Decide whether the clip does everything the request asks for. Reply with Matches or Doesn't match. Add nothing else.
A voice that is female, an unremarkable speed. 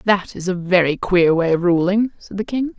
Doesn't match